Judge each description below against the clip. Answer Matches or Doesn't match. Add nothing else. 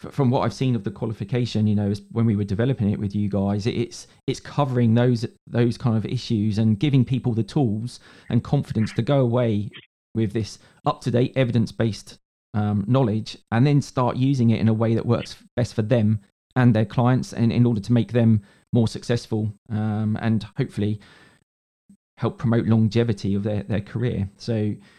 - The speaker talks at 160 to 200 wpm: Matches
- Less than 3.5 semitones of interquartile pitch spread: Matches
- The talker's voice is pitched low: Matches